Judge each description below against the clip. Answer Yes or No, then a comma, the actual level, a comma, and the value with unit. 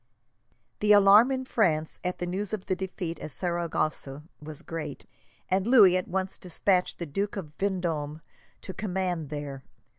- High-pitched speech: No, medium, 180 Hz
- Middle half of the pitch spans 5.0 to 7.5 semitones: No, average, 4.0 semitones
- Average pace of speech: Yes, average, 155 wpm